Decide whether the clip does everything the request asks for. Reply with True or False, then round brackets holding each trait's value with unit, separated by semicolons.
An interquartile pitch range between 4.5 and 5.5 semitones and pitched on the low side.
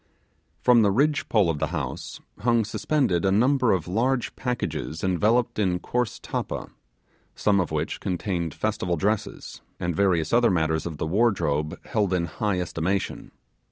True (5.2 semitones; 95 Hz)